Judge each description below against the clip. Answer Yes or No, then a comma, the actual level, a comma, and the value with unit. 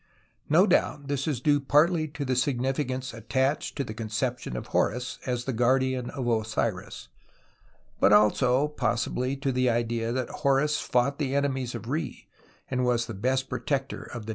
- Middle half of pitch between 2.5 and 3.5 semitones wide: Yes, average, 2.8 semitones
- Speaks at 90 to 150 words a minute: No, average, 175 wpm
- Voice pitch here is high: No, low, 130 Hz